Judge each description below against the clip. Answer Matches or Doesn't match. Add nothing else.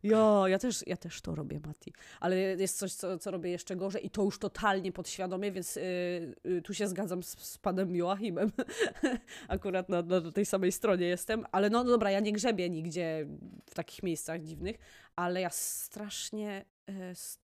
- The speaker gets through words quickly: Matches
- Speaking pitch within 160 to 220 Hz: Matches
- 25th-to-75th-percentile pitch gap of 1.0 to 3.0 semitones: Matches